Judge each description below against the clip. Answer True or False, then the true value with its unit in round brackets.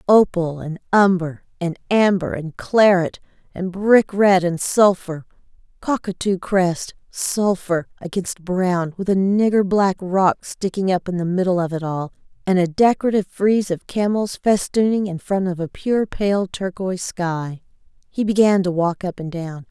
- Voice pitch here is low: False (185 Hz)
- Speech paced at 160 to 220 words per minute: False (150 wpm)